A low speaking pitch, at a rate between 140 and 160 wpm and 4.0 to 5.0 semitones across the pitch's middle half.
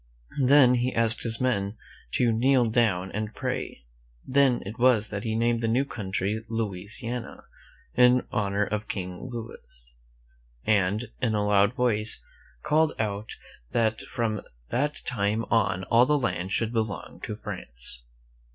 No: low, 110 Hz; average, 150 wpm; average, 3.2 semitones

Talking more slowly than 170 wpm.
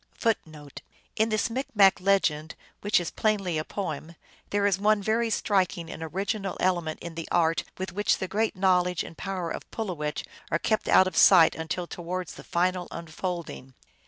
No: average, 175 wpm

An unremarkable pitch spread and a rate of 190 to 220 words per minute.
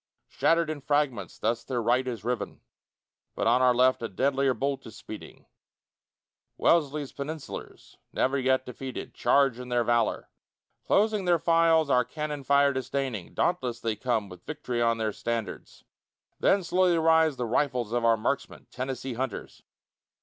No: average, 3.8 semitones; average, 150 wpm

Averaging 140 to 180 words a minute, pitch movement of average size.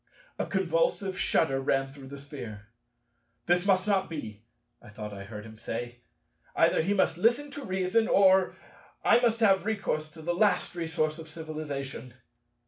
No: average, 160 wpm; wide, 6.4 semitones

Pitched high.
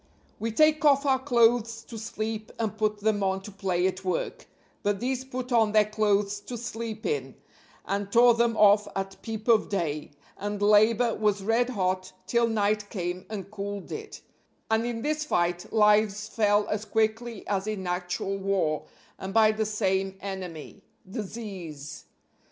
Yes: high, 210 Hz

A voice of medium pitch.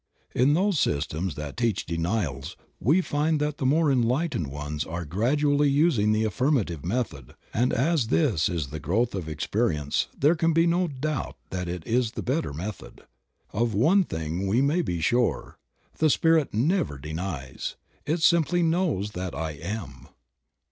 No: low, 115 Hz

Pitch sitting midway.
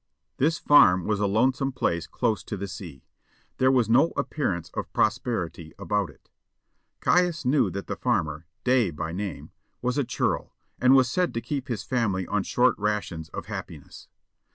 No: low, 110 Hz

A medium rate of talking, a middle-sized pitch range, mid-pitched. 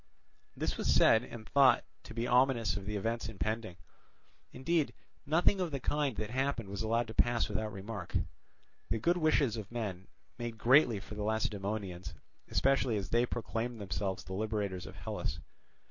No: average, 165 wpm; average, 3.4 semitones; low, 115 Hz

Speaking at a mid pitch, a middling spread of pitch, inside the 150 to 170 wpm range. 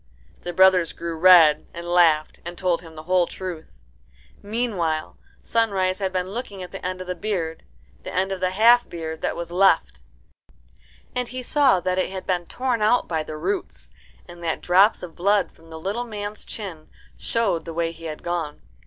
No: medium, 180 Hz; average, 3.4 semitones; average, 190 wpm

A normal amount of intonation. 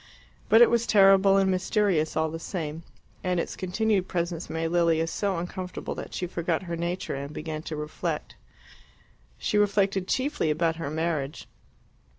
Yes: average, 3.1 semitones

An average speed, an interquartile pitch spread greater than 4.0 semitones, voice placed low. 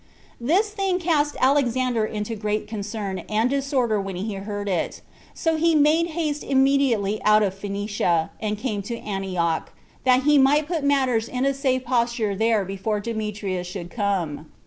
No: average, 160 wpm; wide, 5.4 semitones; high, 225 Hz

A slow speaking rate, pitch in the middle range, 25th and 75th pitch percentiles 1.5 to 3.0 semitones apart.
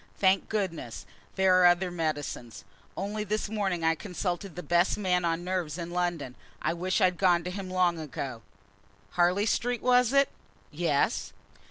No: average, 160 wpm; medium, 180 Hz; narrow, 2.5 semitones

